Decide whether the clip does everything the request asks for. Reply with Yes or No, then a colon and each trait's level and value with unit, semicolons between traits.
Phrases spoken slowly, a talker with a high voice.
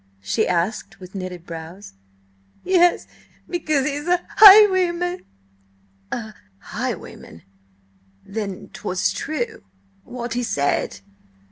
Yes: slow, 95 wpm; high, 240 Hz